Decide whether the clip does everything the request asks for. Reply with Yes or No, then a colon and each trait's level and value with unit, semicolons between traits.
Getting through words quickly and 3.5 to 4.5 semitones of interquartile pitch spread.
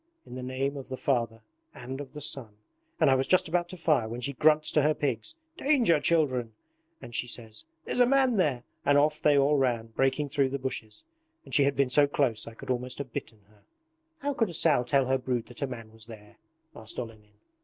Yes: fast, 225 wpm; average, 4.1 semitones